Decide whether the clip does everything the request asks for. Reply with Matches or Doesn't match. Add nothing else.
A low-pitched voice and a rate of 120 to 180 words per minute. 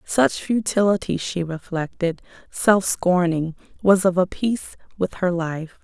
Doesn't match